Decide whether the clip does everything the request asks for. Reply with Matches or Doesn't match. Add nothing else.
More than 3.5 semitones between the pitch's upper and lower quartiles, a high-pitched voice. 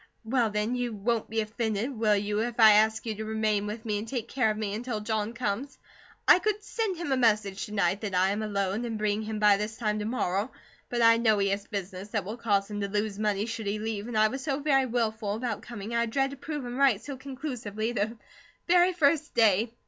Doesn't match